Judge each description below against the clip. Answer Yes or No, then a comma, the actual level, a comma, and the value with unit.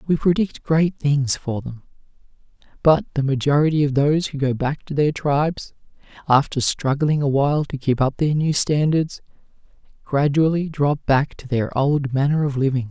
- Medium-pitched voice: Yes, medium, 145 Hz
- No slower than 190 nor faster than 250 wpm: No, average, 165 wpm